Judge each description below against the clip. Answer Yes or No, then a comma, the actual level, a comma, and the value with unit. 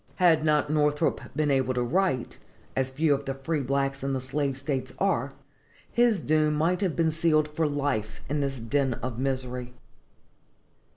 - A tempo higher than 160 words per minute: Yes, average, 170 wpm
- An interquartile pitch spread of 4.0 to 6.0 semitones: No, average, 2.8 semitones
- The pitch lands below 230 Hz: Yes, medium, 140 Hz